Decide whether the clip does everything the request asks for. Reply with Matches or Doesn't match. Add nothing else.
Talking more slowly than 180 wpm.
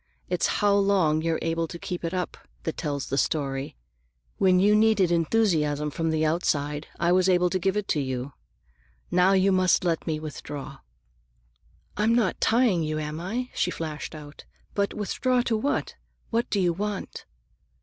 Matches